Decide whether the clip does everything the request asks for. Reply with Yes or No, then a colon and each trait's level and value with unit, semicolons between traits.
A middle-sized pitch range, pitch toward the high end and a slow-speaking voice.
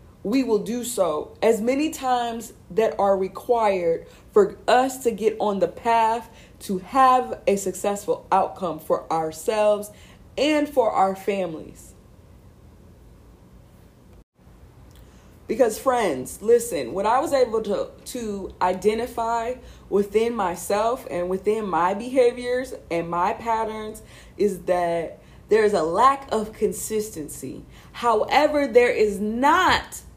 Yes: average, 4.3 semitones; high, 225 Hz; slow, 115 wpm